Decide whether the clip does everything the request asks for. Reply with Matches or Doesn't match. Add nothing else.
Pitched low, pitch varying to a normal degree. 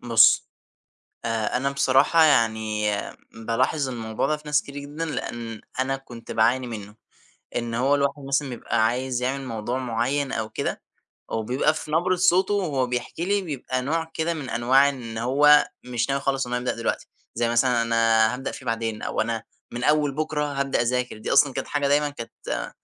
Matches